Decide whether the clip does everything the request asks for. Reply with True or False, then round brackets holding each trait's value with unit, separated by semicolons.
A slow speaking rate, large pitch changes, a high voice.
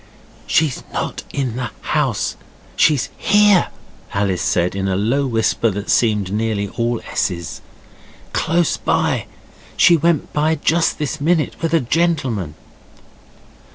False (125 wpm; 7.8 semitones; 125 Hz)